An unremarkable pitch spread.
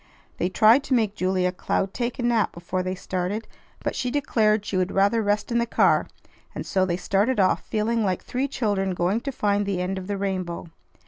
Yes: average, 3.6 semitones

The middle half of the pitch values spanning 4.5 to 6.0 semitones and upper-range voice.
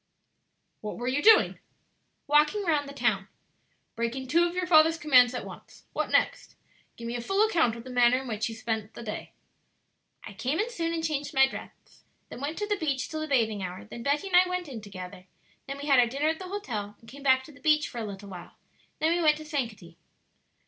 Yes: wide, 5.5 semitones; very high, 270 Hz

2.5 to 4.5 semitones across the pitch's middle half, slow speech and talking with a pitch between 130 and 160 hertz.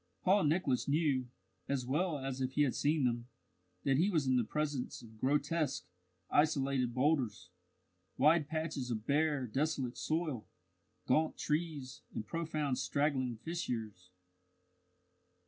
Yes: average, 3.5 semitones; slow, 130 wpm; medium, 140 Hz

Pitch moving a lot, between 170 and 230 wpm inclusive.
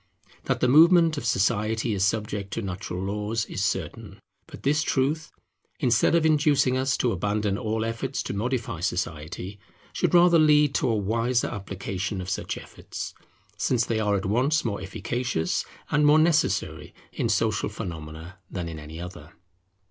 No: wide, 5.7 semitones; average, 160 wpm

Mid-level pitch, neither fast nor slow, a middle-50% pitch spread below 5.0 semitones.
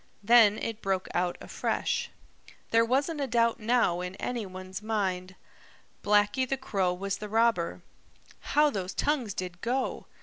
No: high, 210 Hz; average, 145 wpm; average, 4.3 semitones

